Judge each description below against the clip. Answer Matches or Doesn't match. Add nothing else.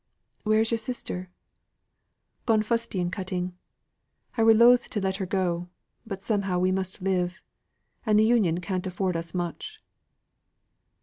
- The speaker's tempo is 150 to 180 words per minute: Doesn't match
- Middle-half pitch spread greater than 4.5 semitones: Doesn't match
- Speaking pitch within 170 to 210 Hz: Matches